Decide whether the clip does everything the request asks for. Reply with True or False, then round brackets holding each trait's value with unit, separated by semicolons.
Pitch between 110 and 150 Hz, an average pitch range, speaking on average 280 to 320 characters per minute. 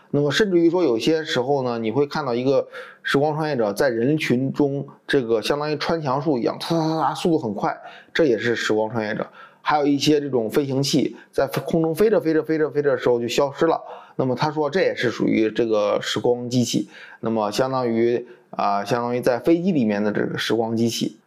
False (140 Hz; 4.8 semitones; 335 characters per minute)